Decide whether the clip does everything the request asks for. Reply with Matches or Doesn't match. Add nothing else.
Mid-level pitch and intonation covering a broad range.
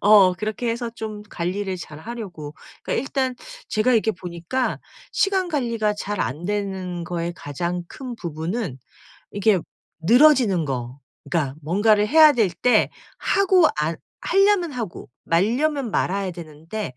Doesn't match